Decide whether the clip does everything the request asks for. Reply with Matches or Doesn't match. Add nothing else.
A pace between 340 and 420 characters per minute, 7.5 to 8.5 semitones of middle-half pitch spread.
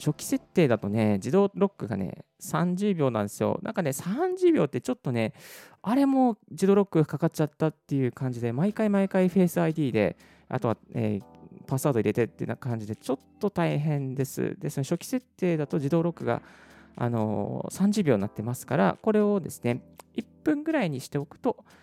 Matches